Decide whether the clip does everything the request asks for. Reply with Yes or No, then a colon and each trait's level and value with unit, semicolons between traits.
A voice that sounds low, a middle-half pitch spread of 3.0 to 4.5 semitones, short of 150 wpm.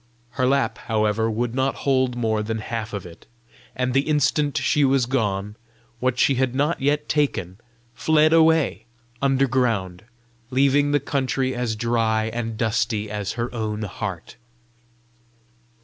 Yes: low, 120 Hz; average, 3.9 semitones; average, 140 wpm